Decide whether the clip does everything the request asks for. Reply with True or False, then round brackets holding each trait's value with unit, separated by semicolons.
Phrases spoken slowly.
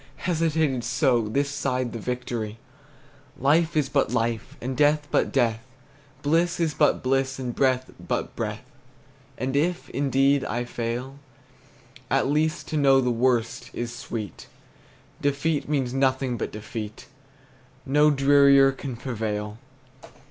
True (130 wpm)